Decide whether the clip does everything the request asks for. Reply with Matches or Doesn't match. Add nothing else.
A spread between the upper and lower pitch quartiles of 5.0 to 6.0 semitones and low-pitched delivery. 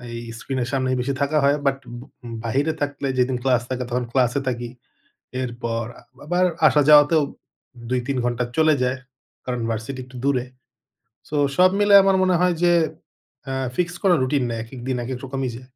Doesn't match